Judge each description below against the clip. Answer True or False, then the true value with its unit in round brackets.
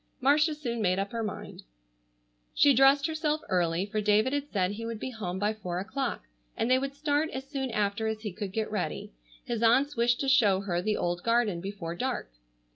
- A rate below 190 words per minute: False (205 wpm)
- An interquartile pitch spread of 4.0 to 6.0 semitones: True (5.3 semitones)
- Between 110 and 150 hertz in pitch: False (225 Hz)